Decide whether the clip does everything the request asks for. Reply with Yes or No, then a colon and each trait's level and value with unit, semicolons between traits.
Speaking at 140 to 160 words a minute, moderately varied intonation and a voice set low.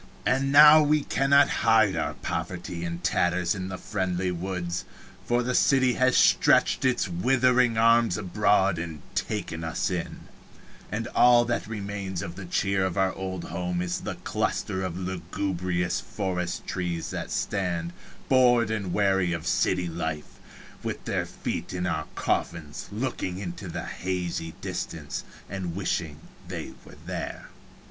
Yes: average, 150 wpm; average, 4.3 semitones; very low, 95 Hz